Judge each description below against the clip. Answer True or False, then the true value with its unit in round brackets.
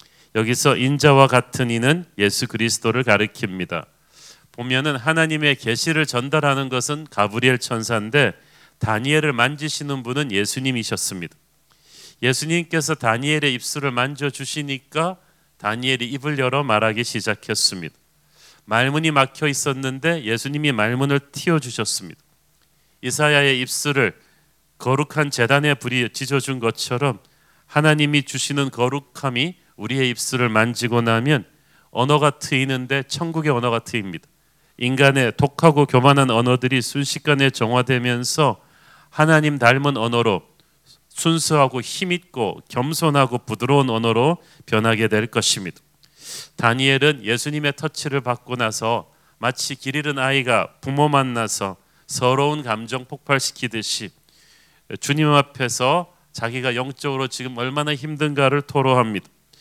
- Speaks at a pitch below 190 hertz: True (135 Hz)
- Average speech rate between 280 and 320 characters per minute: True (305 characters per minute)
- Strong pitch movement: False (3.7 semitones)